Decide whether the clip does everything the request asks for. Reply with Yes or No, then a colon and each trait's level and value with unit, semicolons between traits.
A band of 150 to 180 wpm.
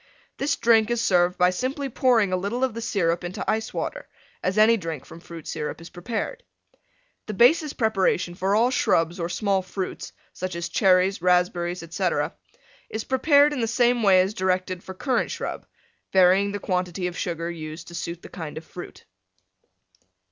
Yes: average, 175 wpm